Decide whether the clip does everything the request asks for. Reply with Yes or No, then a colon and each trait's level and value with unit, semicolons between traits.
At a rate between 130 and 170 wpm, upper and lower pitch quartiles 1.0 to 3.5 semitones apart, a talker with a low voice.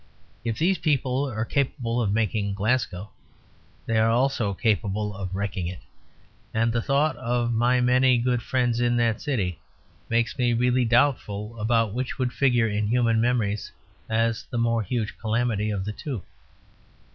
Yes: average, 155 wpm; average, 2.8 semitones; low, 115 Hz